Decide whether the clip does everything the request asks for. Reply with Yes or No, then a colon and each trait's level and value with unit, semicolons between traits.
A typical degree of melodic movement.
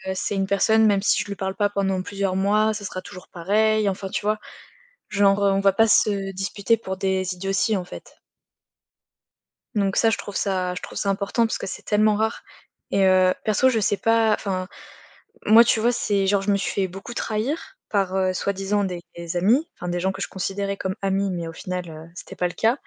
No: narrow, 2.0 semitones